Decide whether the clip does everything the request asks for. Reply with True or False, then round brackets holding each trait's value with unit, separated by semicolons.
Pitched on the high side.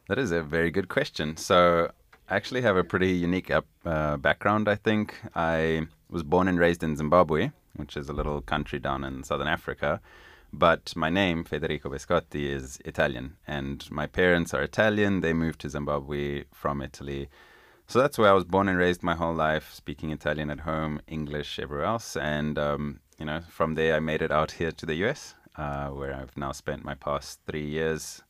False (80 Hz)